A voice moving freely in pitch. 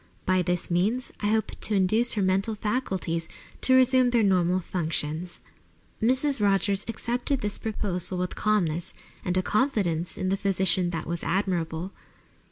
No: average, 3.8 semitones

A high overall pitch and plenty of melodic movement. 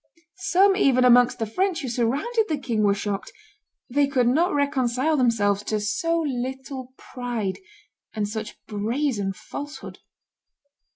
No: very high, 250 Hz; average, 4.9 semitones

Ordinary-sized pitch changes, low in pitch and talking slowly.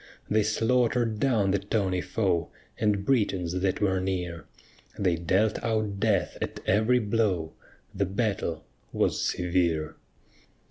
Yes: average, 3.2 semitones; low, 100 Hz; slow, 125 wpm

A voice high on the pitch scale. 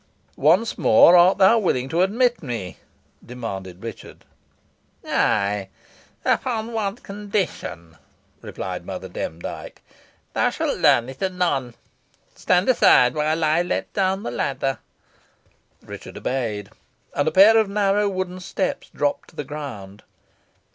No: medium, 160 Hz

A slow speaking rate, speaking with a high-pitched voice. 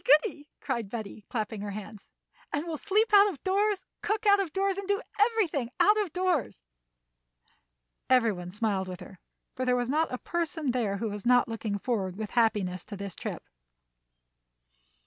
No: average, 175 wpm; very high, 250 Hz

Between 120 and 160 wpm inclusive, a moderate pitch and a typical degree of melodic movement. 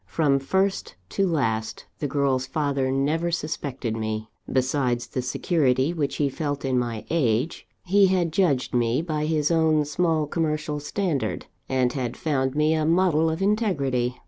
Yes: average, 155 wpm; medium, 145 Hz; average, 3.8 semitones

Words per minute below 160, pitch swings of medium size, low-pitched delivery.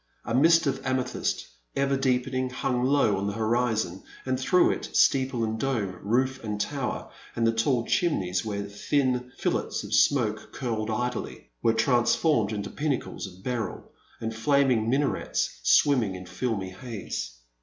Yes: average, 150 wpm; average, 3.4 semitones; low, 120 Hz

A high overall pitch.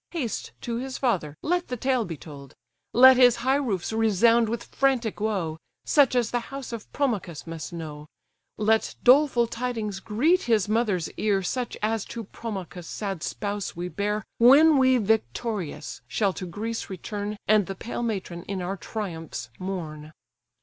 Yes: high, 215 Hz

